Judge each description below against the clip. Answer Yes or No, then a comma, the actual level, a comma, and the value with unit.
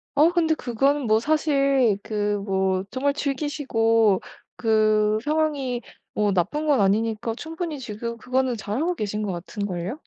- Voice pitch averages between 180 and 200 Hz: No, high, 235 Hz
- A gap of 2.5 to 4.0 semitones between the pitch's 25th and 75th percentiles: No, average, 5.3 semitones